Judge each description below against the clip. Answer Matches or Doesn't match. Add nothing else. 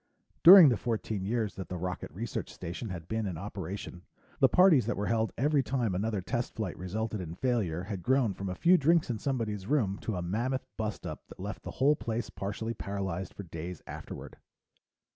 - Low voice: Matches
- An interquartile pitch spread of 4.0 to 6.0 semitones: Matches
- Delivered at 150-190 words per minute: Doesn't match